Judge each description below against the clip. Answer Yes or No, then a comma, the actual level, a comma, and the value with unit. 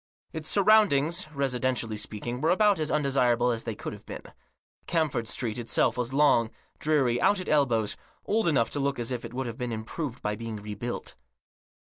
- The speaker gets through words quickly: No, average, 175 wpm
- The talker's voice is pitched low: Yes, low, 125 Hz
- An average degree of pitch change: Yes, average, 4.7 semitones